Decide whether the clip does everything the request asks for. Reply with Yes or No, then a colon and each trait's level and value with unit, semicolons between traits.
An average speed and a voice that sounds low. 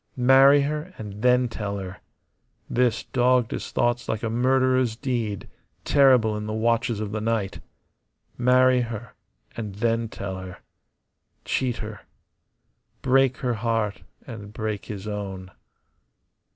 No: slow, 130 wpm; low, 115 Hz